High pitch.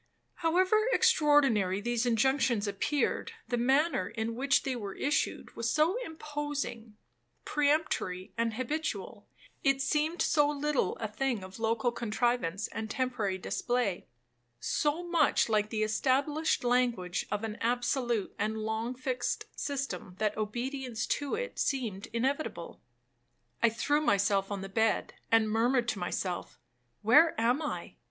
Yes: high, 240 Hz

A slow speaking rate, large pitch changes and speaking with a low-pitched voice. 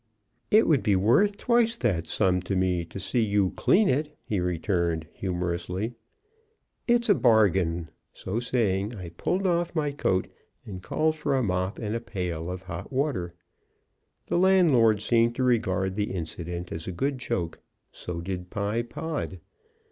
No: average, 160 wpm; wide, 6.9 semitones; low, 105 Hz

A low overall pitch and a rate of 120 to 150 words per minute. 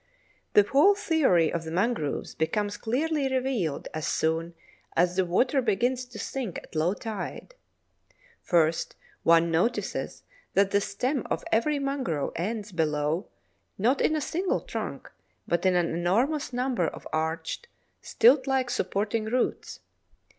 No: high, 210 Hz; average, 140 wpm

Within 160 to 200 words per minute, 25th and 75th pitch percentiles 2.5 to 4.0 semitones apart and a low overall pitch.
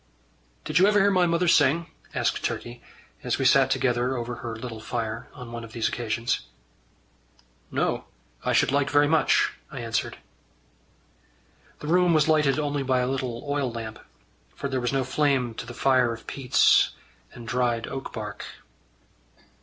Yes: average, 165 wpm; average, 3.6 semitones; low, 130 Hz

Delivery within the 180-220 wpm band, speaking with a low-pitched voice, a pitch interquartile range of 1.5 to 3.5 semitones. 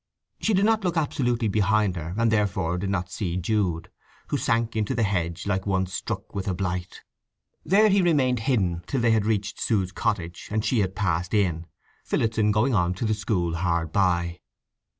No: average, 190 wpm; low, 100 Hz; average, 4.3 semitones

